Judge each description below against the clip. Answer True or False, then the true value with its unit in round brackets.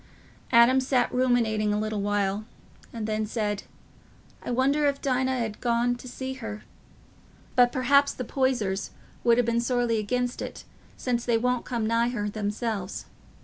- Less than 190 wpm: True (160 wpm)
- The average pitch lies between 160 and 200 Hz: False (235 Hz)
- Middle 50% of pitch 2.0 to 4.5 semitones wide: True (2.8 semitones)